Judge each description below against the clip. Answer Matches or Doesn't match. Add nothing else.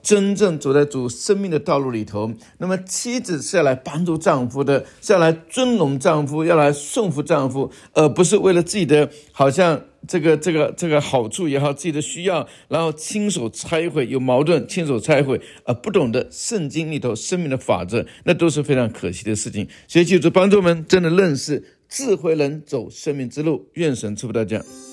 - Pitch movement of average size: Matches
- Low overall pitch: Doesn't match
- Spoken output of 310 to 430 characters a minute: Doesn't match